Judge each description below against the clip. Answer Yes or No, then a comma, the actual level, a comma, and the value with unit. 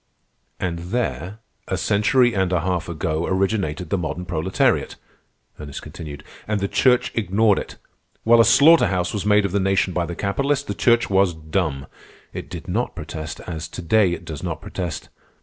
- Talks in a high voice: No, very low, 95 Hz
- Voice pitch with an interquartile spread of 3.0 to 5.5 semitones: Yes, average, 3.9 semitones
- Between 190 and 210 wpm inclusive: No, average, 180 wpm